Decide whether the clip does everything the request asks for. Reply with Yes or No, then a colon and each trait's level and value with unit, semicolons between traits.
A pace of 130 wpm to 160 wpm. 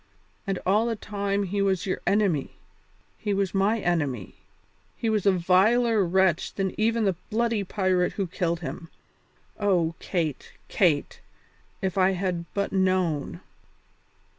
Yes: average, 140 wpm